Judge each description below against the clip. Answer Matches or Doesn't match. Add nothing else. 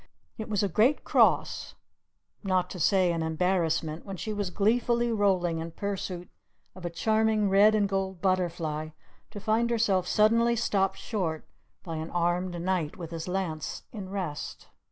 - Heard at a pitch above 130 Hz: Matches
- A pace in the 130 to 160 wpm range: Matches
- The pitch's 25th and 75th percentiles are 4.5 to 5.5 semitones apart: Doesn't match